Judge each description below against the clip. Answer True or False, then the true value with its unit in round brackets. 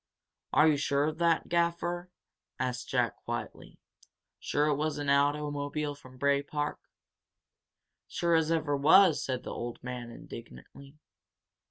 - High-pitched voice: False (145 Hz)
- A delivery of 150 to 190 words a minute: False (140 wpm)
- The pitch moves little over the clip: True (2.3 semitones)